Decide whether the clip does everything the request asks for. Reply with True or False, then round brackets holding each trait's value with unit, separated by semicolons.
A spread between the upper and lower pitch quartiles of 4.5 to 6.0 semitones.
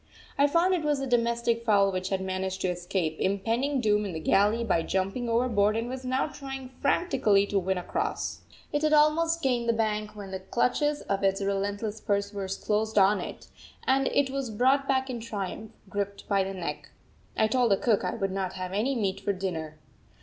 True (4.8 semitones)